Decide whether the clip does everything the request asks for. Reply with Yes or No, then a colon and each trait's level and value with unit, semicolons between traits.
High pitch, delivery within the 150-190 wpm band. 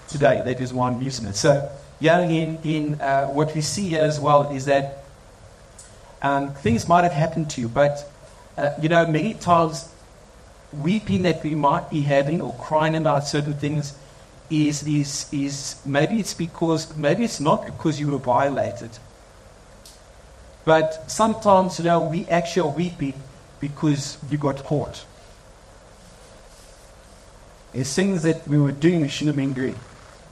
No: medium, 145 Hz; average, 155 wpm